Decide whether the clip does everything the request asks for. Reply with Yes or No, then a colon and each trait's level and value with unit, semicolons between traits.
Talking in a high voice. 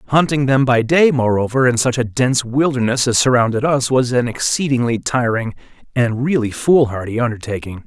No: low, 125 Hz